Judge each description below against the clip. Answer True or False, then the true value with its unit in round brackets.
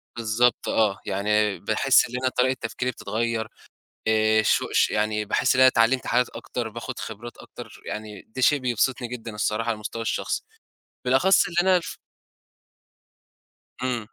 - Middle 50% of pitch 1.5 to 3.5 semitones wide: True (2.7 semitones)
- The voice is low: True (115 Hz)